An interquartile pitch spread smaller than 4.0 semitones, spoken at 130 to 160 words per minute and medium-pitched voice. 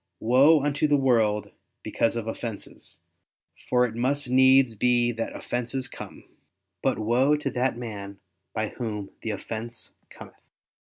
No: average, 2.9 semitones; average, 140 wpm; low, 120 Hz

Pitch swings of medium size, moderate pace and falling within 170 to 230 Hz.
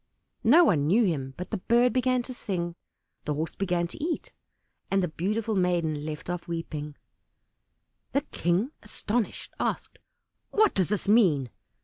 No: wide, 6.1 semitones; average, 150 wpm; medium, 185 Hz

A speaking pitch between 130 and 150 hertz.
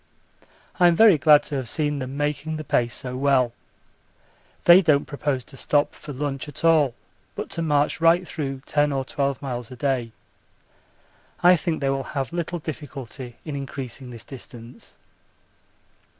Yes: medium, 140 Hz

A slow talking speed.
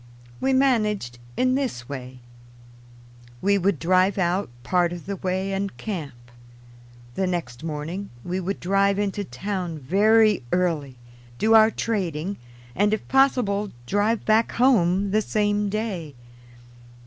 Yes: slow, 130 wpm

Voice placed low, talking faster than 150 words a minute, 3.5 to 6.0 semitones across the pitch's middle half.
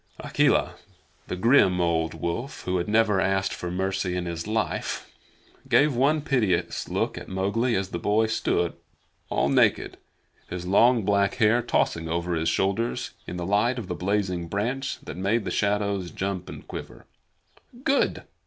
Yes: low, 100 Hz; average, 160 wpm; average, 4.0 semitones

